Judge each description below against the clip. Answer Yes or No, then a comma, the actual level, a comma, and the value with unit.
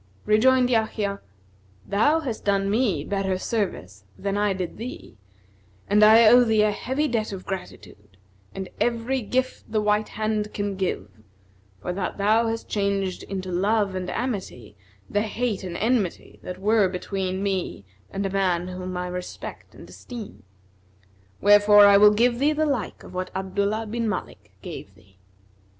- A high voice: Yes, high, 205 Hz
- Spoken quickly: No, average, 160 wpm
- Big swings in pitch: No, average, 3.1 semitones